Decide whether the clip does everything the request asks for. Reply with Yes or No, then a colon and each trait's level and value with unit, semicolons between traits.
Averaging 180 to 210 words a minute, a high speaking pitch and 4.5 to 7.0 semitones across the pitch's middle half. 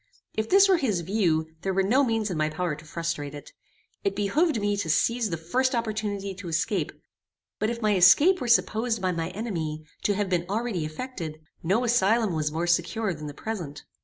Yes: average, 200 wpm; high, 195 Hz; average, 5.2 semitones